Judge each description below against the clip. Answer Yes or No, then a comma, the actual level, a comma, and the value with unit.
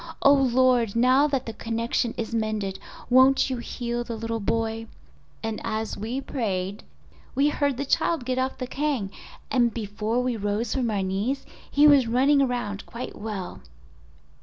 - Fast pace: No, average, 160 wpm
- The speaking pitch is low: No, high, 235 Hz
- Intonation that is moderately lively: Yes, average, 3.0 semitones